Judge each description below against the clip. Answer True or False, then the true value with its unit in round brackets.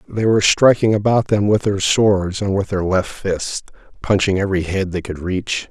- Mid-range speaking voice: False (100 Hz)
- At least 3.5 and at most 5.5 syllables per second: True (4.8 syllables/s)